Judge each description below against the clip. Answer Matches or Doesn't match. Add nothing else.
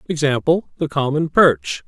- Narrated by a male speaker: Matches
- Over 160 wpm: Doesn't match